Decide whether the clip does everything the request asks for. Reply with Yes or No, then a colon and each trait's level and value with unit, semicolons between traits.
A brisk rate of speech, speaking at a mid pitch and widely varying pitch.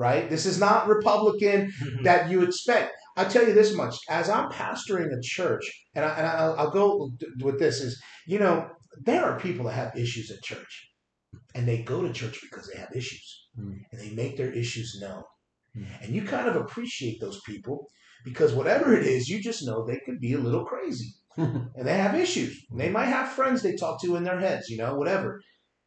Yes: fast, 210 wpm; medium, 160 Hz; wide, 8.6 semitones